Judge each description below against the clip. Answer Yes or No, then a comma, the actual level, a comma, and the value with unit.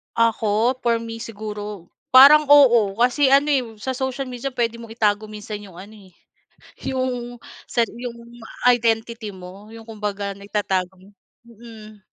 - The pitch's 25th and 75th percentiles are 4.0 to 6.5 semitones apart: No, average, 3.0 semitones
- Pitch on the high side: Yes, high, 225 Hz